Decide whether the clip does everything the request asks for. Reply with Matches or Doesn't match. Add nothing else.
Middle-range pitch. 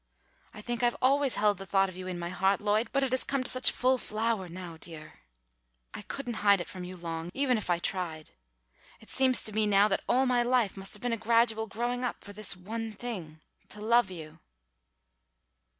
Doesn't match